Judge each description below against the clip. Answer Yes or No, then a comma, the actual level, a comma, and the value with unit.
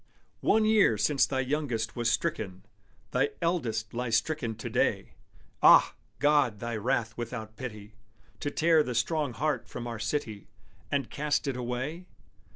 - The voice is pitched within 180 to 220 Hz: No, low, 125 Hz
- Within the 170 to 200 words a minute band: No, average, 155 wpm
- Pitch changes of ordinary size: Yes, average, 4.9 semitones